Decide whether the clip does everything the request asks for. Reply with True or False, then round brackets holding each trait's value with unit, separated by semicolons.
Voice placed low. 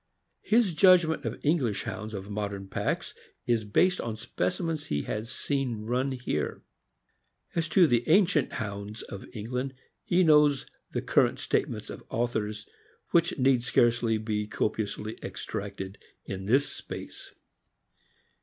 True (120 Hz)